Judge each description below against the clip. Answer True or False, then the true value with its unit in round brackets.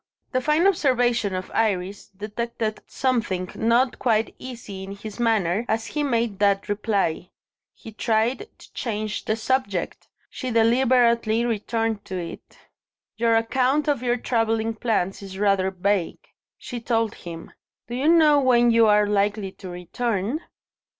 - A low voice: False (225 Hz)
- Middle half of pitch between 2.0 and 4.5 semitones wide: True (3.3 semitones)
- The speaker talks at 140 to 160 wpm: True (145 wpm)